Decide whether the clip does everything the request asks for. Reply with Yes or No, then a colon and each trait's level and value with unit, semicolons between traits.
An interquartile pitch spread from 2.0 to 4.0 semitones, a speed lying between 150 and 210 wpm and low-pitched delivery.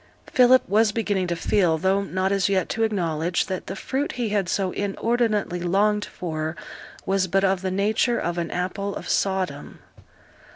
No: average, 2.8 semitones; average, 170 wpm; high, 195 Hz